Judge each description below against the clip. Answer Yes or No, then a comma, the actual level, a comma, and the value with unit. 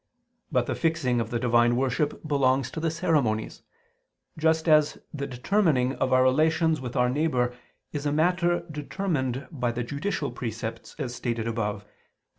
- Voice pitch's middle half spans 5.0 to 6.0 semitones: No, average, 4.5 semitones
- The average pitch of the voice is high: No, low, 135 Hz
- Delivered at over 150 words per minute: Yes, average, 160 wpm